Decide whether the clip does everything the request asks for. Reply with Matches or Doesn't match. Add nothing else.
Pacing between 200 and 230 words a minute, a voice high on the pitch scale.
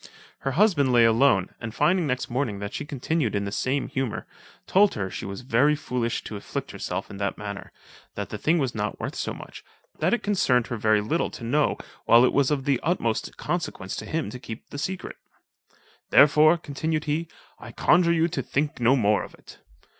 Doesn't match